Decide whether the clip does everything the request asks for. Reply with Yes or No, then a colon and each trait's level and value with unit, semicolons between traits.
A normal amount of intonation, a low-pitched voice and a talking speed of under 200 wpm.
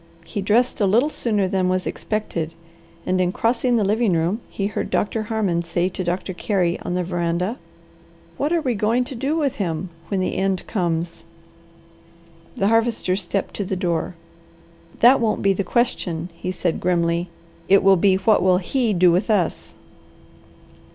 No: average, 4.0 semitones; high, 190 Hz; average, 170 wpm